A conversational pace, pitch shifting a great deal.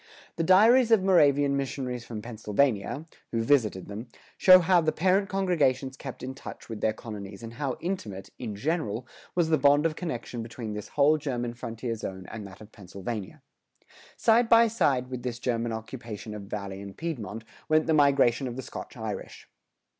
Yes: average, 175 wpm; wide, 6.1 semitones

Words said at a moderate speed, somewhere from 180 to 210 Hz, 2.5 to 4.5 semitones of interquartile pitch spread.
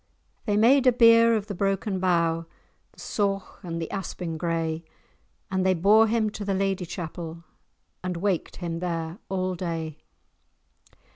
Yes: average, 150 wpm; medium, 185 Hz; average, 3.5 semitones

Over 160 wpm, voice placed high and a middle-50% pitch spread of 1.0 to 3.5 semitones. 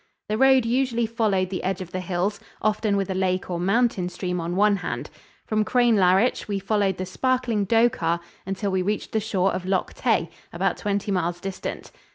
Yes: average, 190 wpm; high, 195 Hz; average, 3.0 semitones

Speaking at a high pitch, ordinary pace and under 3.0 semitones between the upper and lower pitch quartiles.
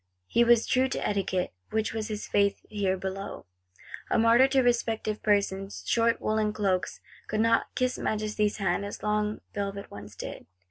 Yes: high, 210 Hz; average, 170 wpm; narrow, 2.4 semitones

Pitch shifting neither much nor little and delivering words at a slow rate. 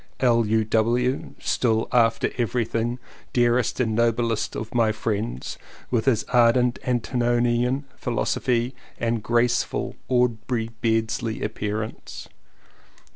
No: narrow, 1.6 semitones; slow, 95 wpm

